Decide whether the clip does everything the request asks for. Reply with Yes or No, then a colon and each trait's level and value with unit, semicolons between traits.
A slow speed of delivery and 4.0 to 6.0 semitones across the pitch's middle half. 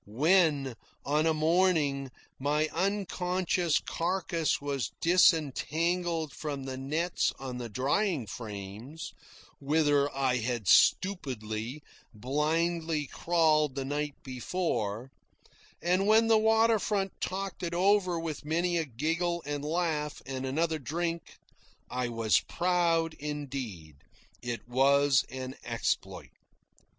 Yes: slow, 110 wpm; average, 4.6 semitones